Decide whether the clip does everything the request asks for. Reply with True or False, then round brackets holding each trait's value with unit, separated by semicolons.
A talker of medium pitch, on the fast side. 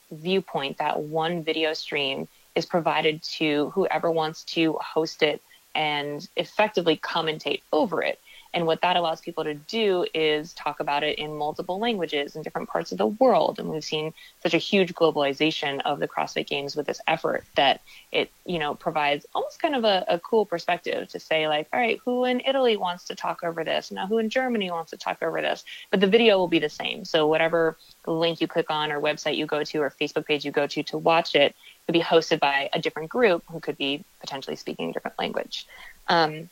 True (160 Hz; 210 wpm)